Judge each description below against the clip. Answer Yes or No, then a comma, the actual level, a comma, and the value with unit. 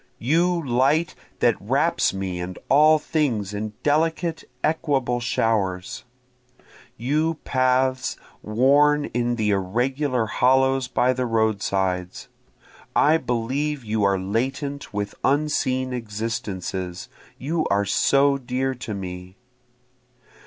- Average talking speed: No, slow, 105 wpm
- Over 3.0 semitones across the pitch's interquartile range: Yes, wide, 5.4 semitones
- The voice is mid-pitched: No, low, 125 Hz